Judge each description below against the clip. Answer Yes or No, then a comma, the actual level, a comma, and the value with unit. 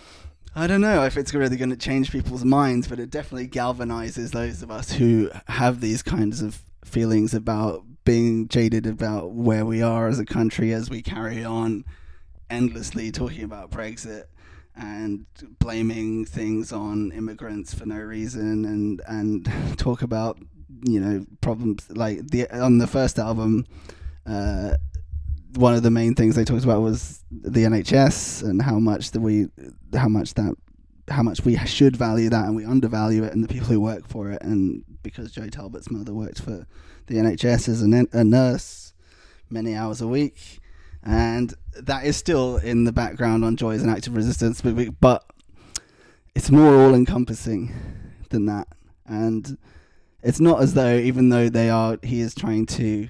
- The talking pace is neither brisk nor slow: Yes, average, 170 wpm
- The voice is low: Yes, low, 110 Hz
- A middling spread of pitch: No, narrow, 2.3 semitones